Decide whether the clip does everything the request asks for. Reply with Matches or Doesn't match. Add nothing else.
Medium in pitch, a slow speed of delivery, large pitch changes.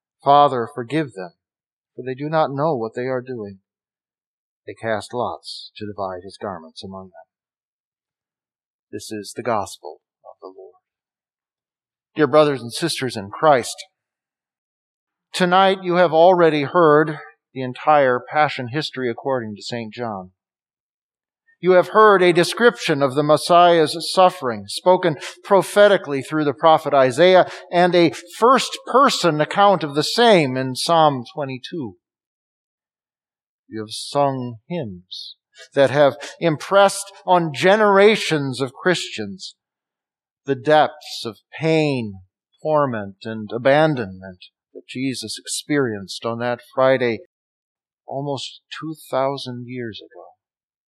Matches